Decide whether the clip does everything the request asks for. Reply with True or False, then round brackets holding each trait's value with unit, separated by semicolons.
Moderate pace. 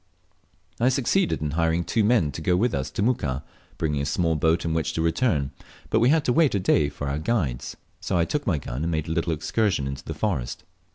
False (235 wpm)